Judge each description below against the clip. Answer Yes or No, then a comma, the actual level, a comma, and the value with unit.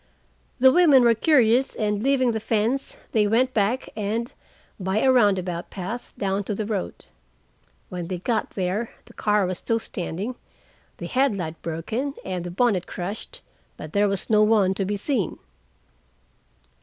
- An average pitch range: Yes, average, 4.2 semitones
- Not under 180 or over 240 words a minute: No, average, 155 wpm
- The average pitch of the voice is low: No, high, 210 Hz